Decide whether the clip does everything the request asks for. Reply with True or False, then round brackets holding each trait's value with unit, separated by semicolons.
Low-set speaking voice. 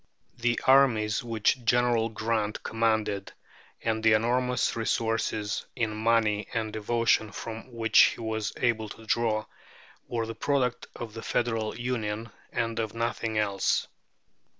True (115 Hz)